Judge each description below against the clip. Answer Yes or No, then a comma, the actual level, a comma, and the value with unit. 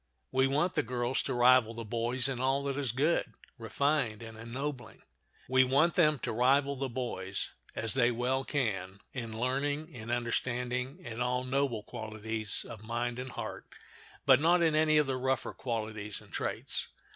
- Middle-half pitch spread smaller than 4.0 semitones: Yes, average, 3.0 semitones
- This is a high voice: No, low, 125 Hz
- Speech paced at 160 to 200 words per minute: Yes, average, 170 wpm